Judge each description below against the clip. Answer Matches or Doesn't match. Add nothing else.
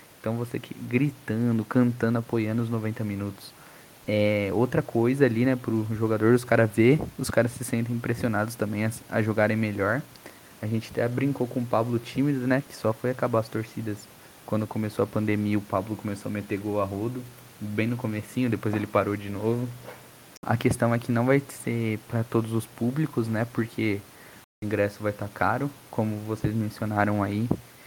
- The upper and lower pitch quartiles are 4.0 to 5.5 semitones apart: Doesn't match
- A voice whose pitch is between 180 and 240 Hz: Doesn't match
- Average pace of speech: Doesn't match